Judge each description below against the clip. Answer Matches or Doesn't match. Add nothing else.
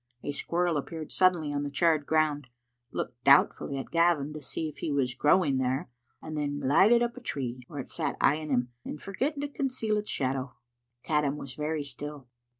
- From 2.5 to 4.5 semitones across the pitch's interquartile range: Matches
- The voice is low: Doesn't match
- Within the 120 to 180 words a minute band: Doesn't match